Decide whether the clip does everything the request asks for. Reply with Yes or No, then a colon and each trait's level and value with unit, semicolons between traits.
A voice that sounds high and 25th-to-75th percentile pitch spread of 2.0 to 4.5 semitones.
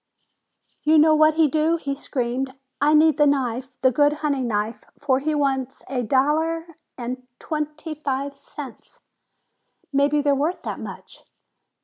Yes: very high, 285 Hz; average, 2.8 semitones